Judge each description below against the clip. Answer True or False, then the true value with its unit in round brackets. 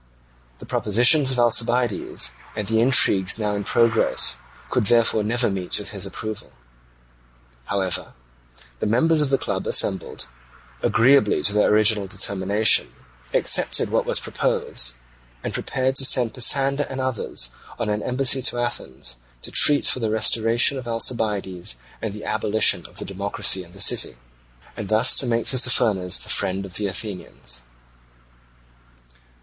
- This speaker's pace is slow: False (145 wpm)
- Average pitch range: True (3.7 semitones)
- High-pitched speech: False (110 Hz)